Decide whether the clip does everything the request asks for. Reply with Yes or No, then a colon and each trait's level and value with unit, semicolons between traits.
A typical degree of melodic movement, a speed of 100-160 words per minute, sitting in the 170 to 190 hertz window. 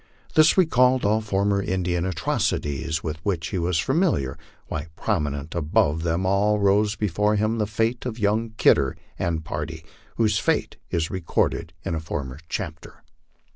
No: average, 4.9 semitones; average, 150 wpm; very low, 95 Hz